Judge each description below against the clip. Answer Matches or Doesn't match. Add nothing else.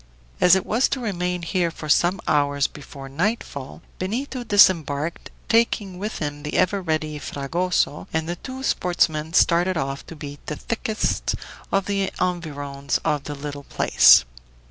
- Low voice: Doesn't match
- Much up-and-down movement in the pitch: Doesn't match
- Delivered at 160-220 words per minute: Doesn't match